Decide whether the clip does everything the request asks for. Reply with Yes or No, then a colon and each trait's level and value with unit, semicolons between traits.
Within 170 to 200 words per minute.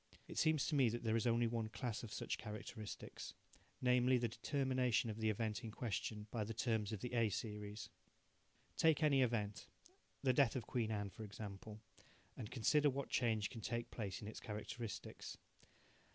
Yes: average, 180 wpm